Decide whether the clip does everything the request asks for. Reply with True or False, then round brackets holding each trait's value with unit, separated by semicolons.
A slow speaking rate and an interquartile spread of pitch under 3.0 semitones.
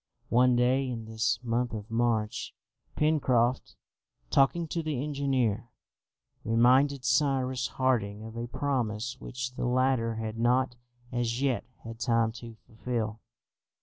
True (125 wpm; 2.4 semitones)